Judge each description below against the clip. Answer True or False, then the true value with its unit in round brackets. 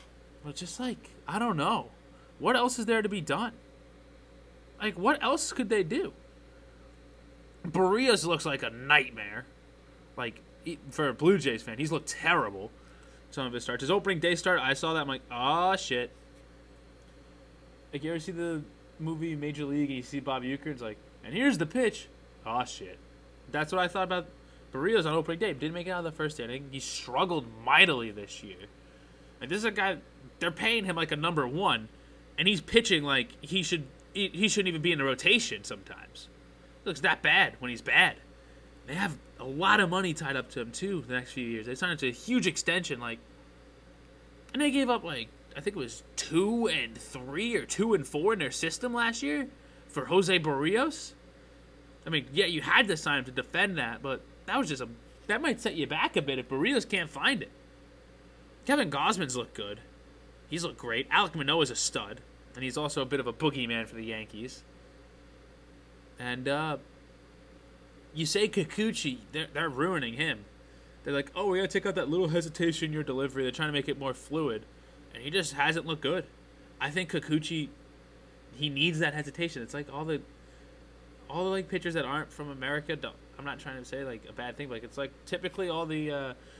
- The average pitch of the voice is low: False (150 Hz)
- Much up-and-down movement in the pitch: True (6.2 semitones)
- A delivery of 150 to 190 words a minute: False (205 wpm)